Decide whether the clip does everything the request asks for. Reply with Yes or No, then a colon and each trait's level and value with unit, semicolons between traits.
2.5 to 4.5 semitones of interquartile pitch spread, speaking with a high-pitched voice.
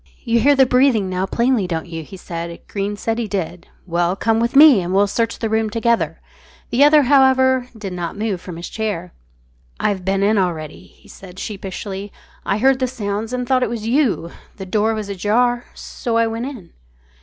Yes: average, 4.2 semitones; high, 215 Hz